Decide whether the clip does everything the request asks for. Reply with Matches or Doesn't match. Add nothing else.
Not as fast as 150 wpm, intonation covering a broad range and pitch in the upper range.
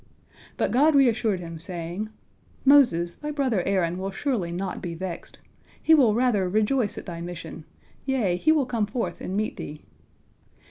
Doesn't match